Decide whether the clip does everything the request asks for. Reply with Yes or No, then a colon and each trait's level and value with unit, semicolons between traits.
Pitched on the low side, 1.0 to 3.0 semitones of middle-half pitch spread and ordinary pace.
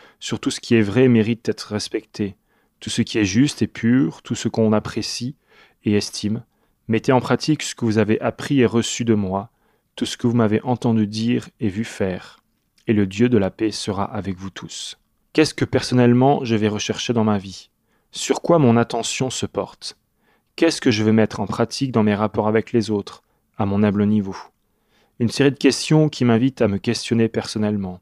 Yes: low, 115 Hz; narrow, 2.5 semitones; average, 210 wpm